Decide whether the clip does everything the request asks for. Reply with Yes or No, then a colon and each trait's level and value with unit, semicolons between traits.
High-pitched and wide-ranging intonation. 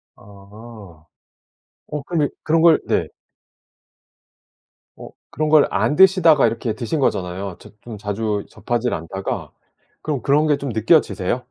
No: low, 125 Hz; wide, 6.6 semitones